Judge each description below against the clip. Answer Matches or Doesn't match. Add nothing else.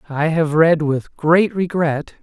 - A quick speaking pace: Doesn't match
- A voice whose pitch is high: Doesn't match